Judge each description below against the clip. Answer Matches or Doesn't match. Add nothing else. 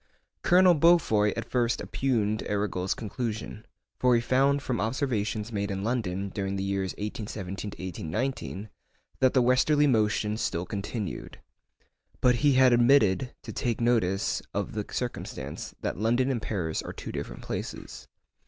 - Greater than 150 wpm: Doesn't match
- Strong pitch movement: Doesn't match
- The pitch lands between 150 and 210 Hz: Doesn't match